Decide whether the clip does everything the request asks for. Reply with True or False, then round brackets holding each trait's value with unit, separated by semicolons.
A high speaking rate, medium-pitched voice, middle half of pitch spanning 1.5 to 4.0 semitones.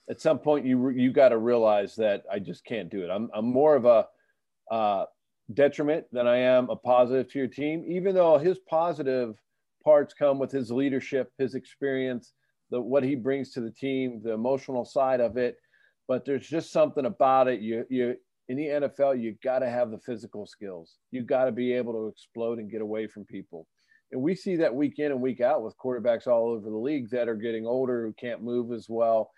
False (215 wpm; 130 Hz; 3.2 semitones)